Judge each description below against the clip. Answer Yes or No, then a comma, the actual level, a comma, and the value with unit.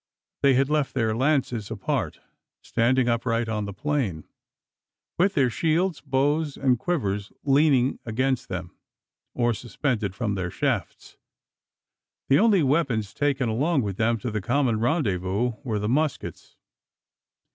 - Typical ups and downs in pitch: Yes, average, 4.8 semitones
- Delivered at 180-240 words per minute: No, slow, 135 wpm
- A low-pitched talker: Yes, low, 125 Hz